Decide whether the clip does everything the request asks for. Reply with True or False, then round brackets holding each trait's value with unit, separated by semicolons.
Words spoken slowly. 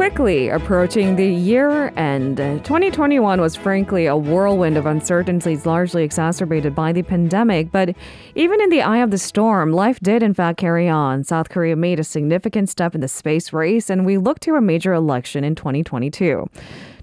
False (175 wpm)